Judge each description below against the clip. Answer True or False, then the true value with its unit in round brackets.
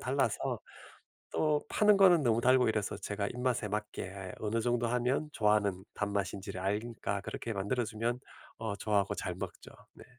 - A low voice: True (110 Hz)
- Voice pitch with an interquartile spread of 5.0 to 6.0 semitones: False (3.4 semitones)